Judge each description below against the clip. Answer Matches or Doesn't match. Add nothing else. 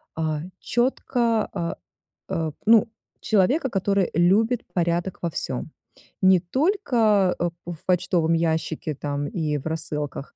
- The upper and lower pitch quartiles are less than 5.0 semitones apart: Doesn't match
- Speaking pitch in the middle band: Matches